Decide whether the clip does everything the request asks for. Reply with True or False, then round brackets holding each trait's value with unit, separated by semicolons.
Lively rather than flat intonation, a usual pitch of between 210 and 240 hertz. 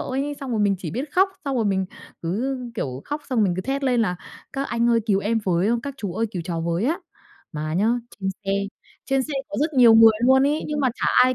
True (6.0 semitones; 230 Hz)